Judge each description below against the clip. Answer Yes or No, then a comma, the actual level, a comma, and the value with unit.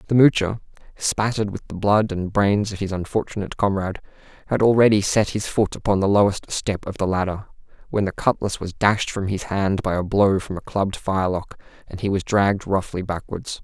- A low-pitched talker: Yes, low, 100 Hz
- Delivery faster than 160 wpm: Yes, average, 200 wpm